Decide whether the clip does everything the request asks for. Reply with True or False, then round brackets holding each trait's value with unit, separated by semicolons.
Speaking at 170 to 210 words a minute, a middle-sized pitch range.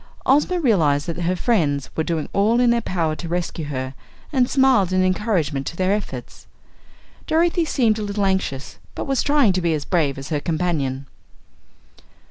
False (175 wpm; 7.2 semitones)